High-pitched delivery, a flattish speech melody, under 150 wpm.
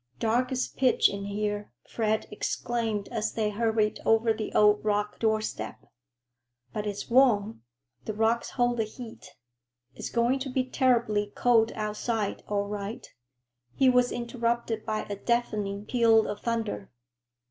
Yes: high, 220 Hz; narrow, 2.2 semitones; average, 140 wpm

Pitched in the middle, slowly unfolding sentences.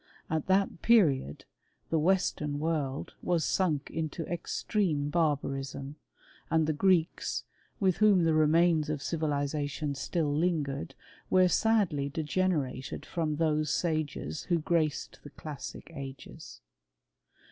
Yes: medium, 155 Hz; slow, 115 wpm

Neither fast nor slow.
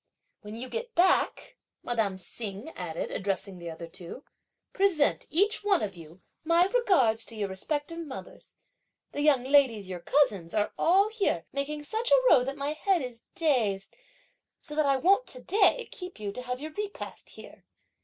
Yes: average, 175 wpm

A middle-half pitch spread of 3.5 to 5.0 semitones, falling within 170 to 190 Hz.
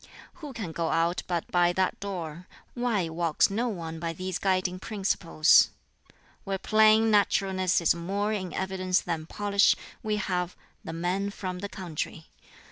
No: average, 3.0 semitones; medium, 185 Hz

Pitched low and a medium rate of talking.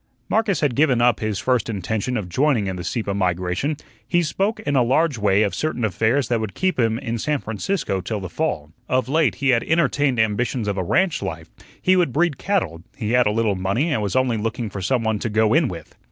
No: low, 115 Hz; fast, 230 wpm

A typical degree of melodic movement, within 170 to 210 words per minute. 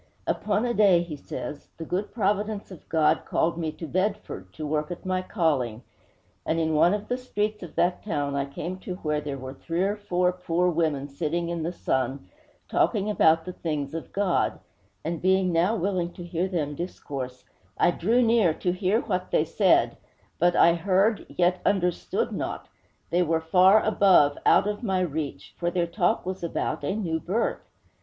Yes: average, 3.3 semitones; average, 185 wpm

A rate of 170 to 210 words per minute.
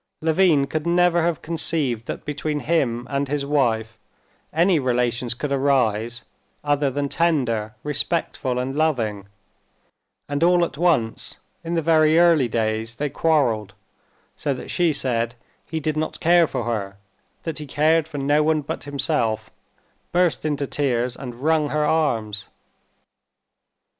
No: average, 145 wpm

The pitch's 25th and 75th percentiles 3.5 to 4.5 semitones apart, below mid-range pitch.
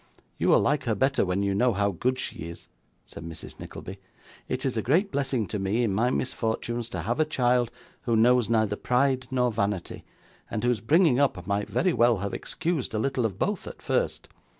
Yes: average, 4.2 semitones; low, 120 Hz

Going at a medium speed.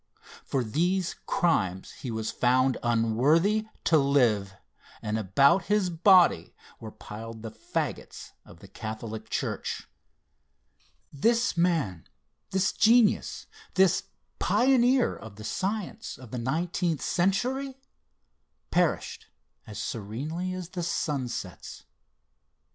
No: slow, 110 wpm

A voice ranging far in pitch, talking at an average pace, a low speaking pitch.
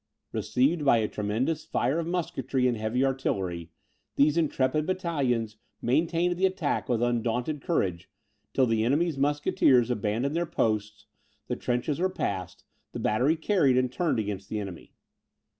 Yes: wide, 6.1 semitones; average, 145 wpm; low, 130 Hz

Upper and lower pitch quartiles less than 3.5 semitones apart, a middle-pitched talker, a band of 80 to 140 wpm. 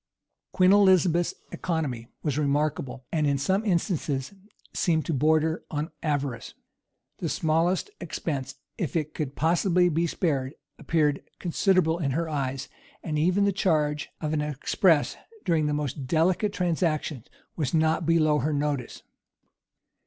Yes: average, 2.8 semitones; medium, 155 Hz; slow, 135 wpm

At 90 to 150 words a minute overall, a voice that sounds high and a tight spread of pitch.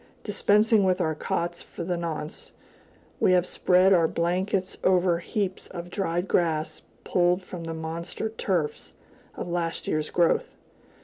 No: average, 140 wpm; medium, 175 Hz; narrow, 2.0 semitones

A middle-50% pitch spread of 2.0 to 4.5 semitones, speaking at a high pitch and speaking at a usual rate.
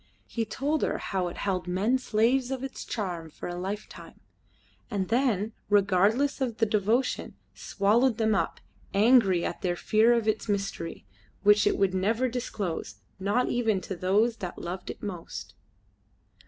Yes: average, 3.9 semitones; high, 210 Hz; average, 155 wpm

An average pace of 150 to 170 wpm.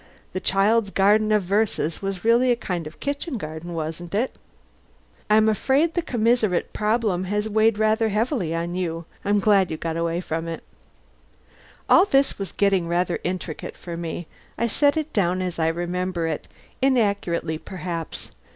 Yes: average, 160 wpm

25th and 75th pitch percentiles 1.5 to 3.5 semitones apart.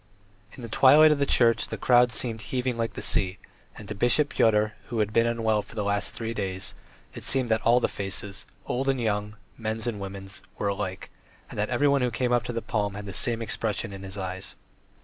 Yes: average, 3.1 semitones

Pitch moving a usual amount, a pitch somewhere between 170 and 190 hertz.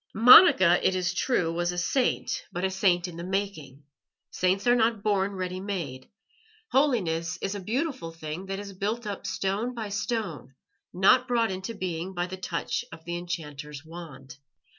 Yes: average, 3.5 semitones; medium, 185 Hz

